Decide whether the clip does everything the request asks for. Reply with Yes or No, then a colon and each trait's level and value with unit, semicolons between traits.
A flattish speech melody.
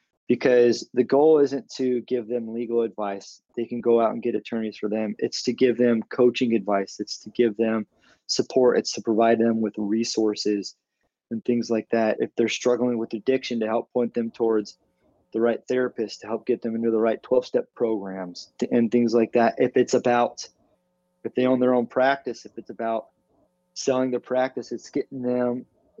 Yes: narrow, 1.9 semitones